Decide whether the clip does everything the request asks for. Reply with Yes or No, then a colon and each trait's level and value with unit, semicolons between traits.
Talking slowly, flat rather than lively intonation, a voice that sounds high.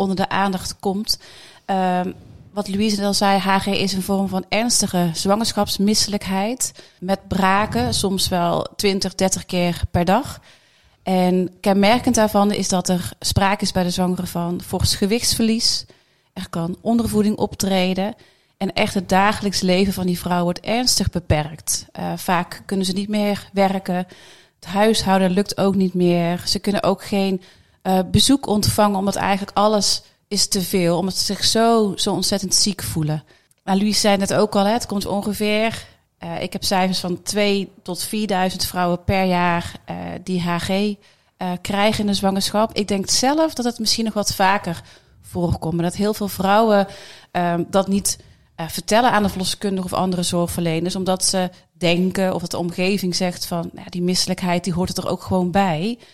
No: average, 175 wpm; narrow, 2.1 semitones; high, 195 Hz